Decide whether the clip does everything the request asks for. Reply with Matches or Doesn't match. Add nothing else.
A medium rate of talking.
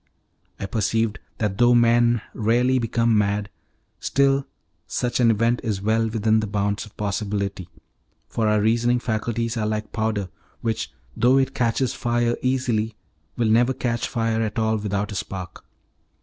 Matches